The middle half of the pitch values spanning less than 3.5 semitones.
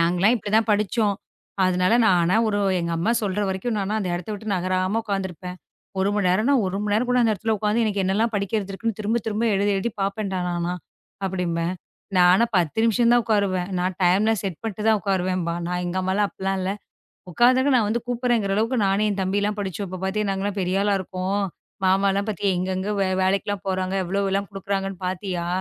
Yes: narrow, 2.4 semitones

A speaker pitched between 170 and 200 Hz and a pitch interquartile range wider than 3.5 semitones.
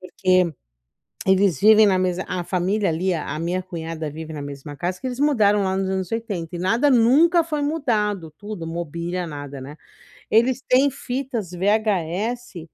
Yes: high, 190 Hz; average, 5.1 semitones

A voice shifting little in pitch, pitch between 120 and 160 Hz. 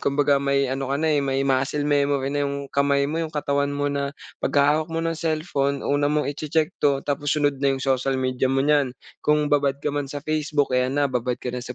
Yes: narrow, 1.4 semitones; medium, 140 Hz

